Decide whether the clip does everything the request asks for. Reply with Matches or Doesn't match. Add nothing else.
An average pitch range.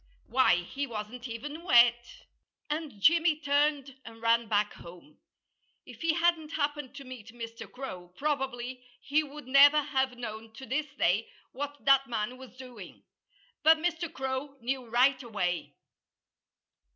Matches